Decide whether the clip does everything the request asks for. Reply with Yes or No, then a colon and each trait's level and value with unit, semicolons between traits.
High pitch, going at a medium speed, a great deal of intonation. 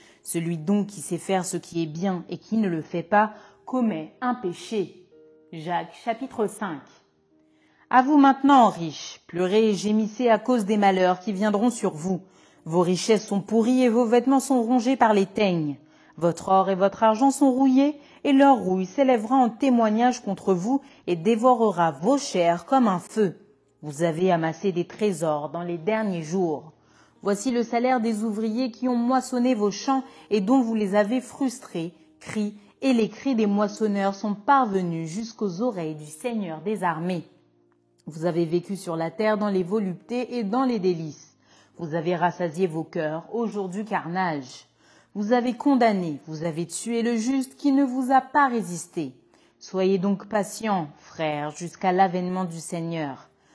Yes: high, 200 Hz; average, 170 wpm; wide, 5.7 semitones